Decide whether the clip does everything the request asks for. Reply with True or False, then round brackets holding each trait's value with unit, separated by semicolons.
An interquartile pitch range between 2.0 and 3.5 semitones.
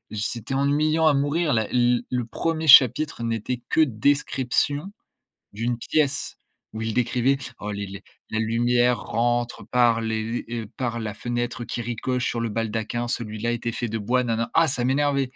True (2.9 semitones)